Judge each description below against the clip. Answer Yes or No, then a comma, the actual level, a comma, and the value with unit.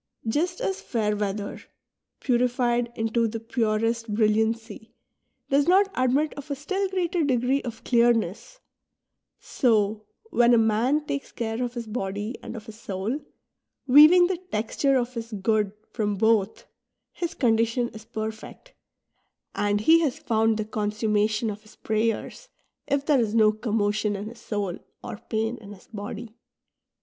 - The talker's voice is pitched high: Yes, high, 225 Hz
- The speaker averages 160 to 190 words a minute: No, average, 150 wpm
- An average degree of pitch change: Yes, average, 3.0 semitones